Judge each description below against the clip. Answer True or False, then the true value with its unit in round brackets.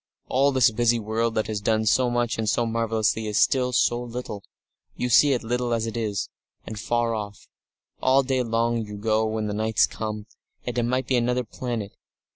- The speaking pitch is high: False (115 Hz)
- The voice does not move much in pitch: True (2.1 semitones)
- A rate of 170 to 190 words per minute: False (205 wpm)